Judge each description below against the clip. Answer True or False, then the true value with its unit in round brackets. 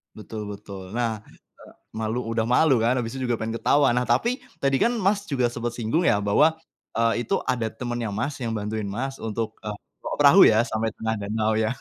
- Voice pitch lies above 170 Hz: False (115 Hz)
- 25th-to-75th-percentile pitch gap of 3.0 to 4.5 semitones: False (2.6 semitones)